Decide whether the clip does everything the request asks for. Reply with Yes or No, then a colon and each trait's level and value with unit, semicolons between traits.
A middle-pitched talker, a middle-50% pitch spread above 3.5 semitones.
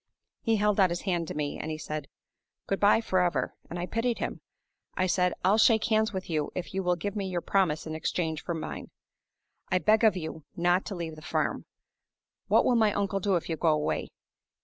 Yes: medium, 180 Hz; average, 3.9 semitones